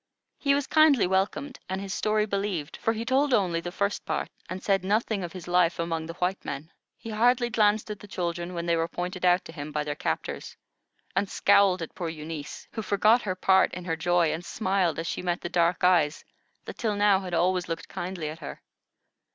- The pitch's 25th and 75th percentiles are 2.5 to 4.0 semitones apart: Yes, average, 3.5 semitones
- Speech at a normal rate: No, fast, 215 wpm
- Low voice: No, medium, 185 Hz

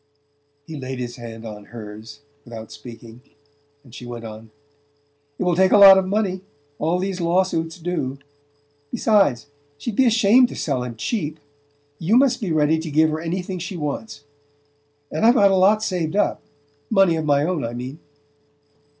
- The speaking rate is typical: Yes, average, 175 wpm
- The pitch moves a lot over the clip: Yes, wide, 7.4 semitones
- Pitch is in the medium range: Yes, medium, 160 Hz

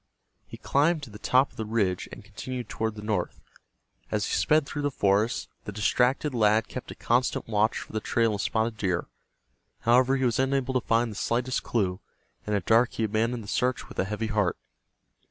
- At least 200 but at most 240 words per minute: Yes, fast, 205 wpm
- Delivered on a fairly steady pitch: No, average, 3.3 semitones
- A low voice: Yes, low, 115 Hz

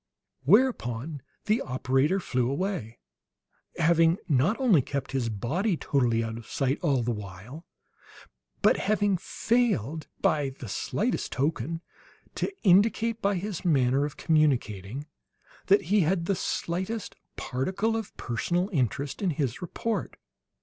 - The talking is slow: Yes, slow, 130 wpm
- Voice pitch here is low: No, medium, 155 Hz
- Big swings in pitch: Yes, wide, 7.1 semitones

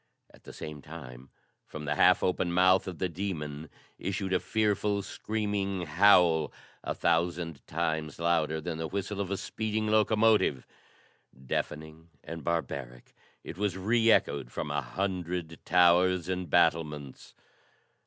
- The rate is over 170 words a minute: No, slow, 135 wpm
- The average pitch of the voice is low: Yes, very low, 85 Hz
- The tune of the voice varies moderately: Yes, average, 3.8 semitones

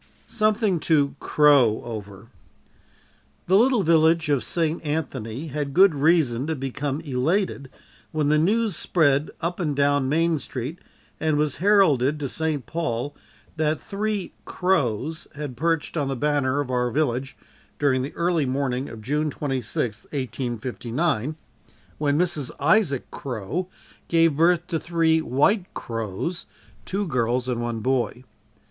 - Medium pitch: Yes, medium, 145 Hz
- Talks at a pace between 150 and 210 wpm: No, slow, 135 wpm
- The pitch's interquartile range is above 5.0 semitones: No, average, 4.4 semitones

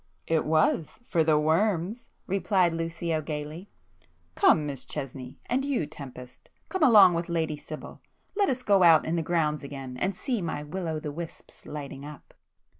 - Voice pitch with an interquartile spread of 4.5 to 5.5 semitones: No, average, 4.0 semitones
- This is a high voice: No, medium, 160 Hz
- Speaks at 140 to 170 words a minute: Yes, average, 150 wpm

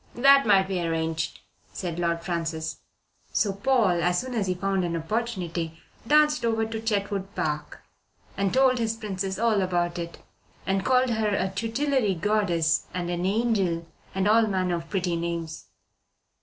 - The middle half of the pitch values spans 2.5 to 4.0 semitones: No, average, 4.5 semitones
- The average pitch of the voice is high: Yes, high, 195 Hz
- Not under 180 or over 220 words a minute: No, average, 155 wpm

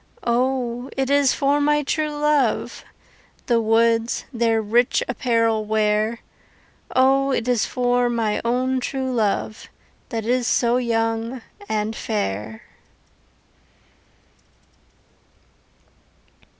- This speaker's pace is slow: Yes, slow, 100 wpm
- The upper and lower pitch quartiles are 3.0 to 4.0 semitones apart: No, narrow, 2.5 semitones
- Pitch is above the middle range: Yes, high, 235 Hz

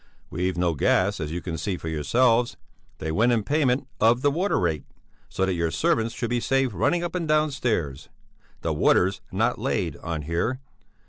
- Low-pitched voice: Yes, low, 105 Hz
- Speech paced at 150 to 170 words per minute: No, average, 190 wpm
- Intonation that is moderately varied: No, wide, 7.5 semitones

